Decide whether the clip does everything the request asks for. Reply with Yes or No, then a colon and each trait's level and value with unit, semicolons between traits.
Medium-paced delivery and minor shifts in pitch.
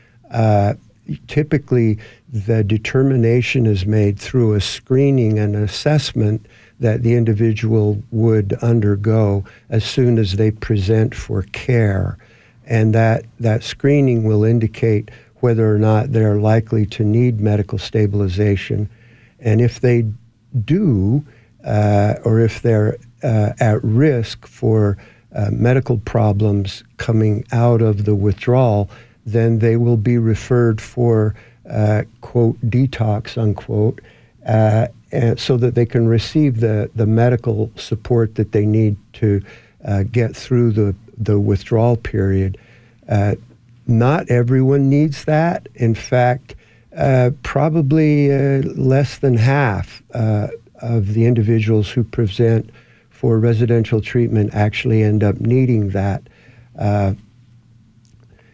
No: slow, 120 wpm; narrow, 2.2 semitones